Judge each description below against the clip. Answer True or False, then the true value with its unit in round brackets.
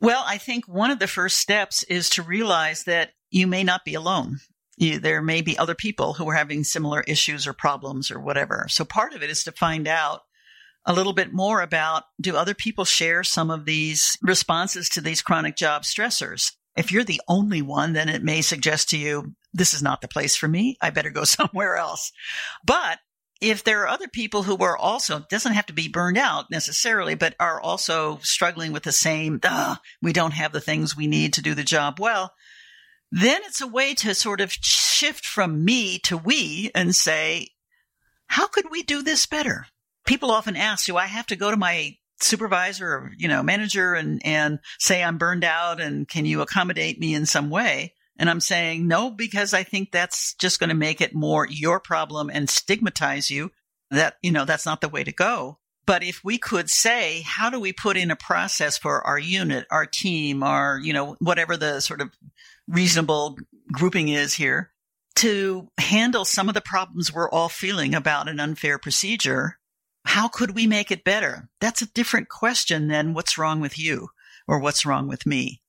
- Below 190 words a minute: False (200 wpm)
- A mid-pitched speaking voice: True (175 Hz)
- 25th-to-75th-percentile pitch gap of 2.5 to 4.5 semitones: False (4.9 semitones)